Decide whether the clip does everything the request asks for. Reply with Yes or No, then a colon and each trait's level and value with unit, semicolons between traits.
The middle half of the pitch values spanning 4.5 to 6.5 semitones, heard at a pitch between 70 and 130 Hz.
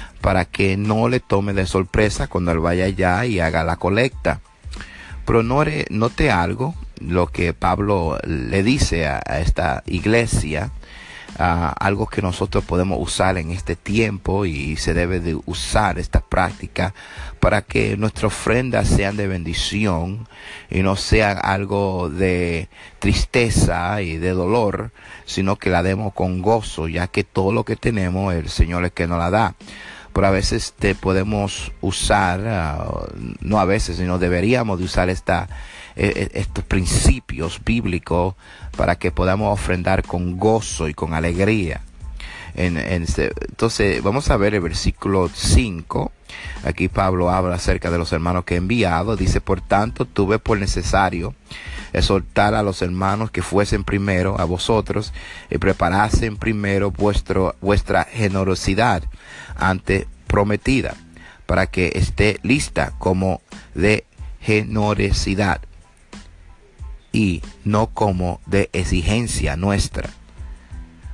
No: average, 2.8 semitones; very low, 95 Hz